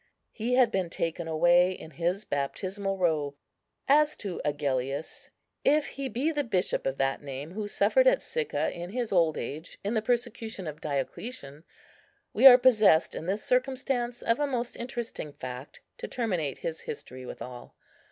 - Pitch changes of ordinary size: No, wide, 8.2 semitones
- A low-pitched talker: No, high, 190 Hz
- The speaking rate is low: No, average, 160 wpm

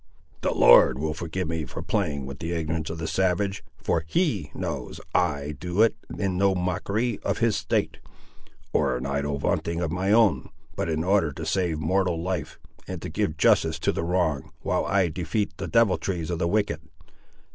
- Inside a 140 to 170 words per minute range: No, average, 185 wpm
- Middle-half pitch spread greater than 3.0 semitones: Yes, average, 3.5 semitones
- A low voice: Yes, very low, 85 Hz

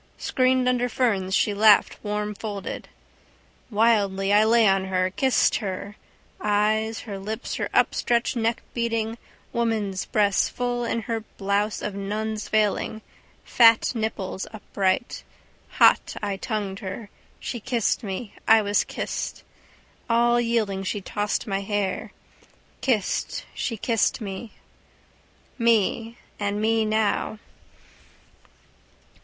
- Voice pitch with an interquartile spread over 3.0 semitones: No, narrow, 2.4 semitones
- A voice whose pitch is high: Yes, high, 215 Hz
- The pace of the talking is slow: Yes, slow, 115 wpm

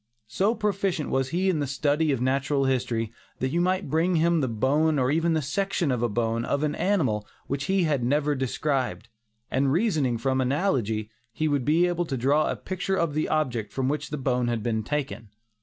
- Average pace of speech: No, fast, 215 wpm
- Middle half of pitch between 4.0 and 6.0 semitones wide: Yes, average, 4.4 semitones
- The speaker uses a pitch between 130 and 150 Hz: Yes, medium, 140 Hz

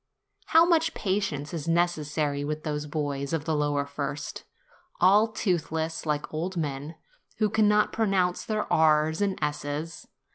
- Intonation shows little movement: No, average, 4.5 semitones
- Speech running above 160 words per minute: No, average, 145 wpm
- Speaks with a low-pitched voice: No, medium, 160 Hz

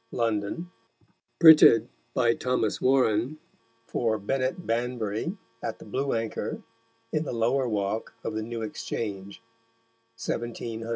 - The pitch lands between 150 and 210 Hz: No, low, 115 Hz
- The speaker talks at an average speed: No, slow, 115 wpm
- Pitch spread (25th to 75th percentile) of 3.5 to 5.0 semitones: No, average, 2.8 semitones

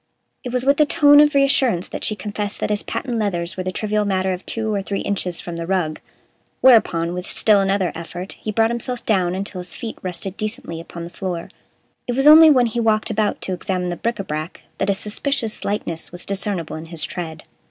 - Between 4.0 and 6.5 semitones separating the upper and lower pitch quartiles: Yes, average, 4.3 semitones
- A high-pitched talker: Yes, high, 200 Hz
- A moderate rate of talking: No, fast, 220 wpm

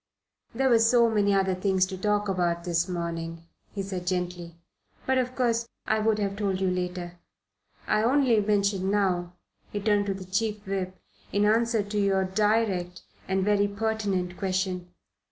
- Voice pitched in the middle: No, high, 195 Hz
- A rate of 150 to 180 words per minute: Yes, average, 170 wpm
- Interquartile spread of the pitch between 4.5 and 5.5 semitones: No, narrow, 2.6 semitones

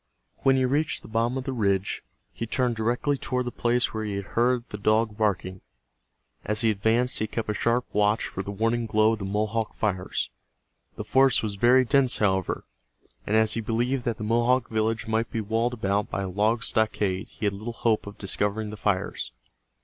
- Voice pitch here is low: Yes, low, 110 Hz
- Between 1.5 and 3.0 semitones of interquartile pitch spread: Yes, narrow, 2.4 semitones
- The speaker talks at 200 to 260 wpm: Yes, fast, 205 wpm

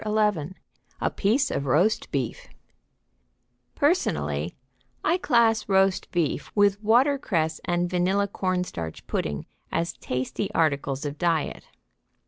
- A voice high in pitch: No, medium, 180 Hz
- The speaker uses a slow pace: Yes, slow, 110 wpm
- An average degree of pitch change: No, wide, 6.5 semitones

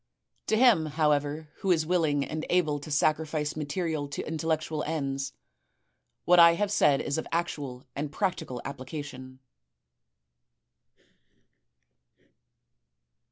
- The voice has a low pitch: No, medium, 155 Hz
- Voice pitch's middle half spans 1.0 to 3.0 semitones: Yes, narrow, 2.4 semitones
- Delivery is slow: Yes, slow, 110 wpm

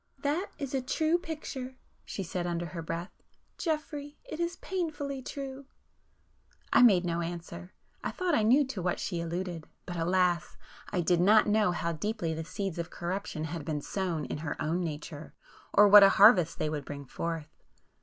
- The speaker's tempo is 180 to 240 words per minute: No, average, 170 wpm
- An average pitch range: No, wide, 7.7 semitones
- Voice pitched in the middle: Yes, medium, 180 Hz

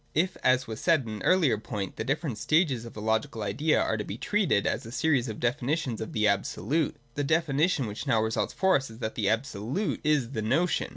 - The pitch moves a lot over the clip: Yes, wide, 5.8 semitones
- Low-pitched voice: Yes, low, 125 Hz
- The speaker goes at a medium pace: No, fast, 225 wpm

